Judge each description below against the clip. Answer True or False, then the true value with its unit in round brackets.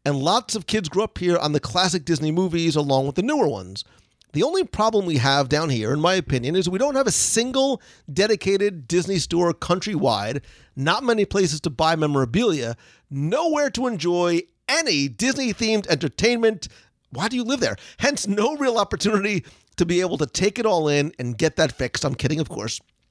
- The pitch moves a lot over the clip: True (6.2 semitones)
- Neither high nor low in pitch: True (175 Hz)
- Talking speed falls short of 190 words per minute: False (195 wpm)